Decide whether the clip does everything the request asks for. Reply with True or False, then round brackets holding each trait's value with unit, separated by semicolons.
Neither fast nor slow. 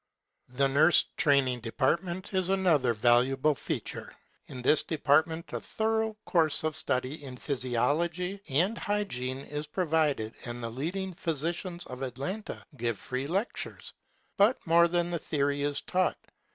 True (145 wpm)